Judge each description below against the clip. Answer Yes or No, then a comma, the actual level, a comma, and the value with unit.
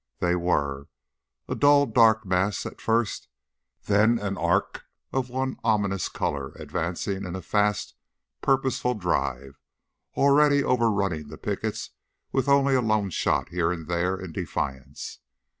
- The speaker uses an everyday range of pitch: No, wide, 6.0 semitones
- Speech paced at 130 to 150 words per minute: Yes, average, 140 wpm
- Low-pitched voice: Yes, low, 100 Hz